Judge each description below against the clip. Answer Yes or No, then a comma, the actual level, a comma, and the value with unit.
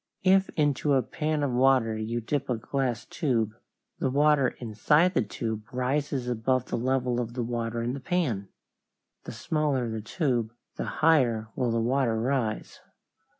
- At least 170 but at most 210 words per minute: No, average, 160 wpm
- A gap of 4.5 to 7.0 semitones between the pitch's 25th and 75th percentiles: No, average, 3.7 semitones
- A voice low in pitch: Yes, low, 125 Hz